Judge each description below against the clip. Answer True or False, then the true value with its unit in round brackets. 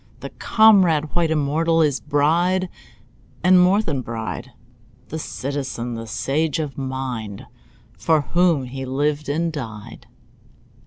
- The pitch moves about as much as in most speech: True (4.0 semitones)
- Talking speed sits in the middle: False (120 wpm)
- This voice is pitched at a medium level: True (150 Hz)